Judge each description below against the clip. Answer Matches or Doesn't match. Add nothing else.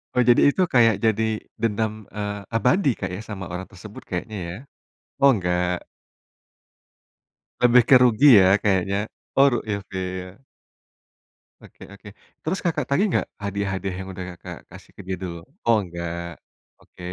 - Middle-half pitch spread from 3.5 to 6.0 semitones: Matches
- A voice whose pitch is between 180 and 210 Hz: Doesn't match